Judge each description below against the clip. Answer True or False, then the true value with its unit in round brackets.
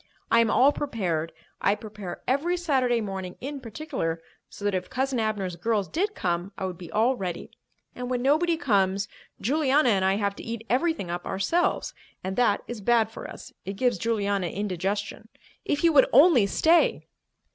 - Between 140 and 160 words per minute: False (175 wpm)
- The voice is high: True (220 Hz)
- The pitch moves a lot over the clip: True (5.7 semitones)